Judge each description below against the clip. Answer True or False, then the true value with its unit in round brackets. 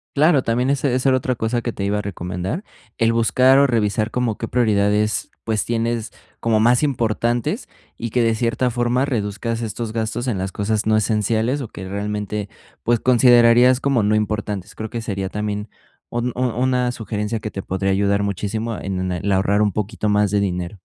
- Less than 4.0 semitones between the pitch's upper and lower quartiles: True (2.7 semitones)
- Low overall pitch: True (110 Hz)